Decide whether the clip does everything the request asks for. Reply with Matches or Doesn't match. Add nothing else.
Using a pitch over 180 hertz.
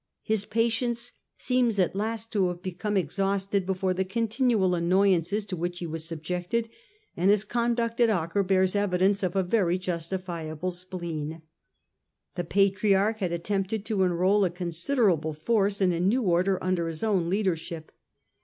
Matches